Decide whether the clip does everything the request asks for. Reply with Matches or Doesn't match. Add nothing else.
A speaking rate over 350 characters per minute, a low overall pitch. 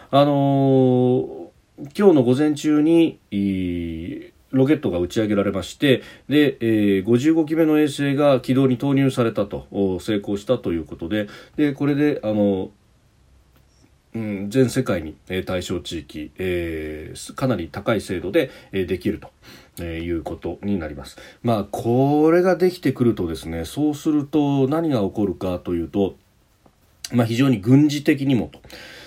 Doesn't match